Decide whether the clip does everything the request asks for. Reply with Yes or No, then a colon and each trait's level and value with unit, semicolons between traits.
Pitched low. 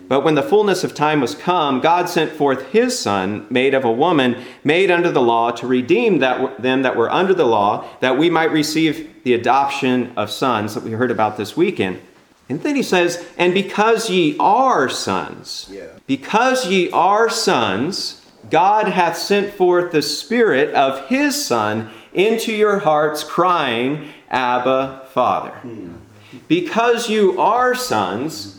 No: medium, 155 Hz